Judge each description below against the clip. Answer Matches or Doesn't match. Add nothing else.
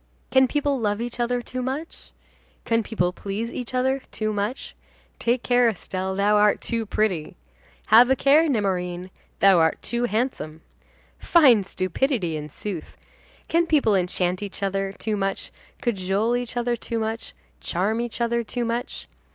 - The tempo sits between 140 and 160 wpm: Matches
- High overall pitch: Matches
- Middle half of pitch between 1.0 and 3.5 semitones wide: Doesn't match